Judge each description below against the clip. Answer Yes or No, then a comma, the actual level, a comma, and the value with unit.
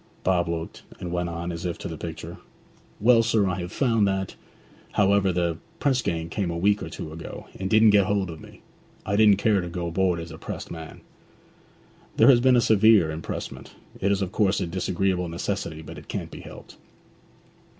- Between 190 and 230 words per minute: Yes, average, 200 wpm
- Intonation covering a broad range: No, average, 3.3 semitones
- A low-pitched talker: Yes, very low, 95 Hz